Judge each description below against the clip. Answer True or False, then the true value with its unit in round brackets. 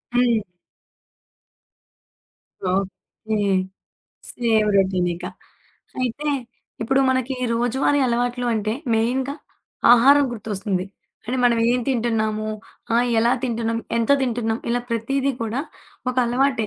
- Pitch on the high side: True (235 Hz)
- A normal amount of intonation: False (2.3 semitones)